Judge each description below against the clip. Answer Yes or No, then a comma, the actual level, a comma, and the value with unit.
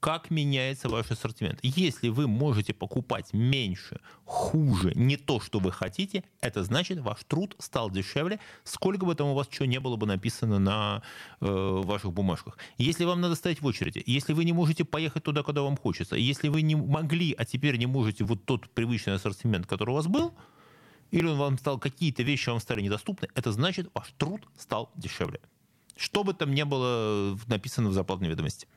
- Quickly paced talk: Yes, fast, 190 wpm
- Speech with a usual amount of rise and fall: No, wide, 6.3 semitones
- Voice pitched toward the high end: No, low, 130 Hz